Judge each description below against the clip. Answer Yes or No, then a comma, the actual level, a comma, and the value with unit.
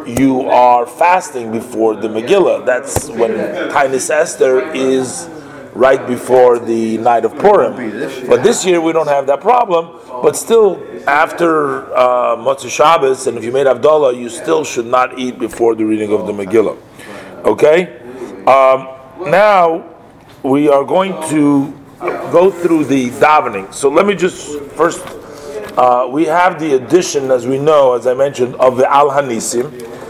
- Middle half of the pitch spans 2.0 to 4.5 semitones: No, average, 5.1 semitones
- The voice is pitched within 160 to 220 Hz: No, low, 135 Hz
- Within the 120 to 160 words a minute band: Yes, average, 155 wpm